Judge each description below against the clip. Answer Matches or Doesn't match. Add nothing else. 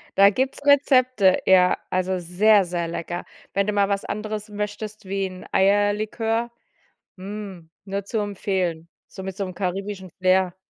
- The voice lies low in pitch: Doesn't match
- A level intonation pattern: Matches